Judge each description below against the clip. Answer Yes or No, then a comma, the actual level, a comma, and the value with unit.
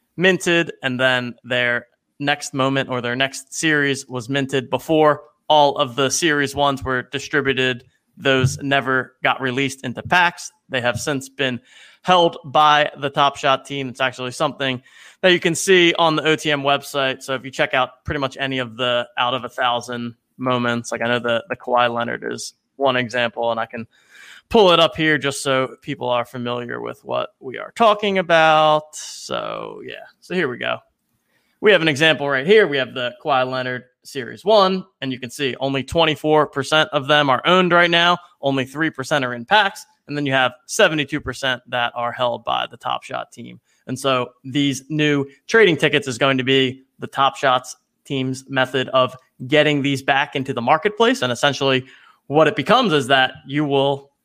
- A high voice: No, low, 135 Hz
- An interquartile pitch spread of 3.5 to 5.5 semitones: No, average, 2.9 semitones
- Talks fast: No, average, 190 wpm